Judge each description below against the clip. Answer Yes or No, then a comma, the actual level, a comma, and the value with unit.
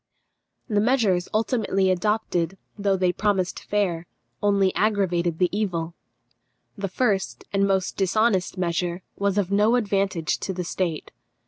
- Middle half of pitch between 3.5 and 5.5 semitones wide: No, narrow, 2.5 semitones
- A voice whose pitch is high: Yes, high, 195 Hz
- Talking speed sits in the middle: No, slow, 130 wpm